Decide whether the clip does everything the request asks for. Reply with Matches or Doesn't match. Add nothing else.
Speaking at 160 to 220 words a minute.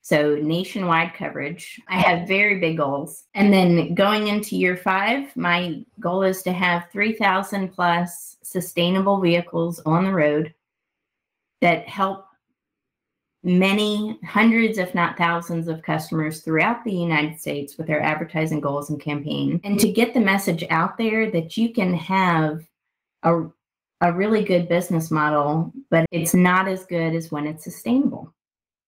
Doesn't match